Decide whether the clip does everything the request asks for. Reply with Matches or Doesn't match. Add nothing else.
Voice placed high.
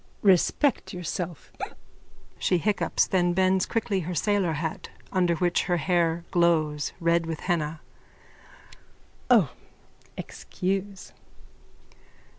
Doesn't match